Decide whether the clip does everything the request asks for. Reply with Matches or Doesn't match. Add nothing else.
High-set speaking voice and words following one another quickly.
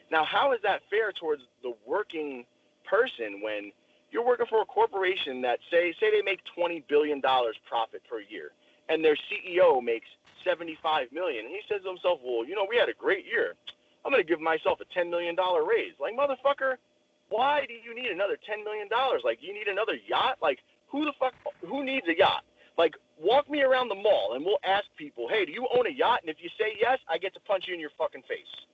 Matches